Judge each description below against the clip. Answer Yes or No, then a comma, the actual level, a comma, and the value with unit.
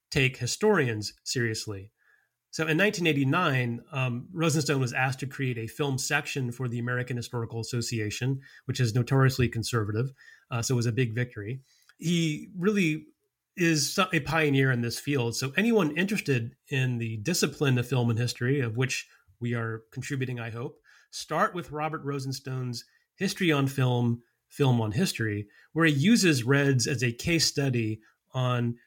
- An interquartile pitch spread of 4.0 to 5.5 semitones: Yes, average, 4.3 semitones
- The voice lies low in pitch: Yes, low, 130 Hz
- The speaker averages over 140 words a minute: Yes, average, 155 wpm